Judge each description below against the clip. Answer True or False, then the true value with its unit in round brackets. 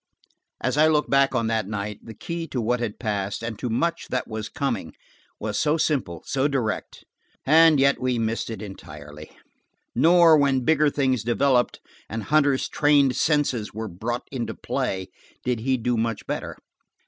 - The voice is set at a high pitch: False (125 Hz)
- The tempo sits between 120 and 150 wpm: False (165 wpm)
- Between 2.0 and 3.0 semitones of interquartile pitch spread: False (4.4 semitones)